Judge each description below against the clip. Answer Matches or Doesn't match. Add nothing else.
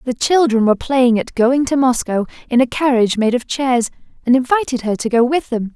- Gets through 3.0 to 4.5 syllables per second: Doesn't match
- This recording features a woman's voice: Matches